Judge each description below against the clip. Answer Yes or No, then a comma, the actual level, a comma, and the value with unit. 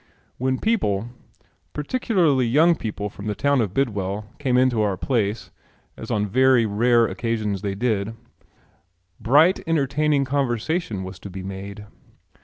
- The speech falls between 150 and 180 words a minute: No, slow, 135 wpm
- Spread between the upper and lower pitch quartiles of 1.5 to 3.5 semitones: No, average, 5.2 semitones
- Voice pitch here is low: Yes, low, 115 Hz